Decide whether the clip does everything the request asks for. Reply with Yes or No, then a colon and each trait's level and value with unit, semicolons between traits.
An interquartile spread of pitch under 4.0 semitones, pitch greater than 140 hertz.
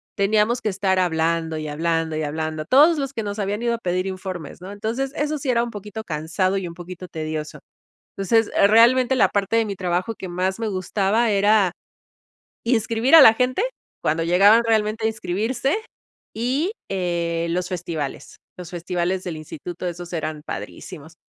No: average, 4.7 semitones; high, 190 Hz